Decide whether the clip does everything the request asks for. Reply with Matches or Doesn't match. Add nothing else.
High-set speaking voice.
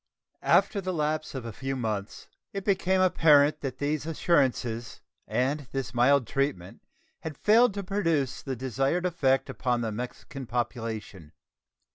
Doesn't match